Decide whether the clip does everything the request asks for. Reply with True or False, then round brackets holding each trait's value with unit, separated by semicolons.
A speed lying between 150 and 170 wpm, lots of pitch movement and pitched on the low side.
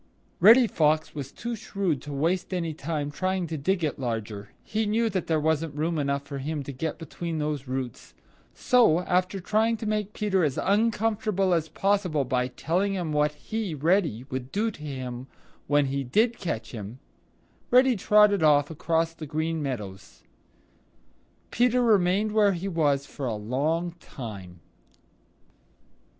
False (155 wpm; 6.0 semitones; 160 Hz)